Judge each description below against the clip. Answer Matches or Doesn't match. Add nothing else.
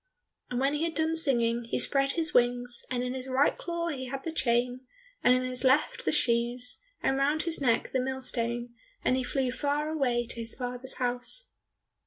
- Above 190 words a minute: Matches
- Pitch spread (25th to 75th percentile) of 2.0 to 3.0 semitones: Matches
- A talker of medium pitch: Doesn't match